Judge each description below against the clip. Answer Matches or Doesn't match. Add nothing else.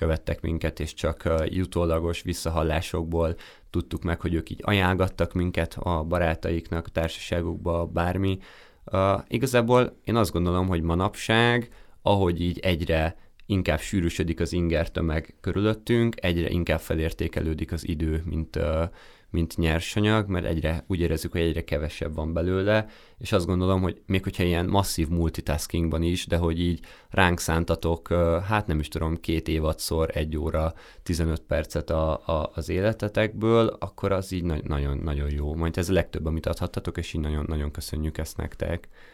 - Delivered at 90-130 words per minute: Doesn't match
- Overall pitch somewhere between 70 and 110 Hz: Matches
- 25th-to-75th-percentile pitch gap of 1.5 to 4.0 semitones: Matches